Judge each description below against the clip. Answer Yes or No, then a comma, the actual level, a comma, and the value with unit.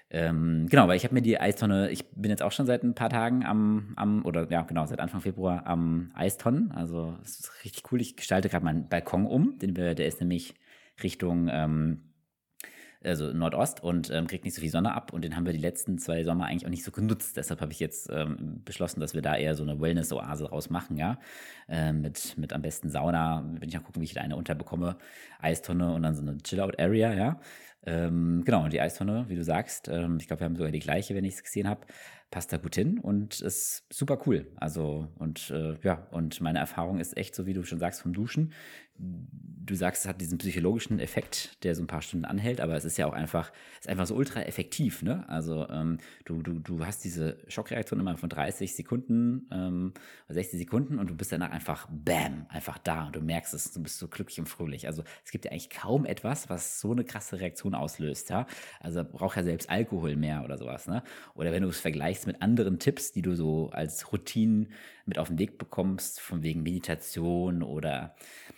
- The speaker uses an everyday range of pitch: Yes, average, 3.0 semitones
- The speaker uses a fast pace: Yes, fast, 220 wpm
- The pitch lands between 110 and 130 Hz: No, very low, 85 Hz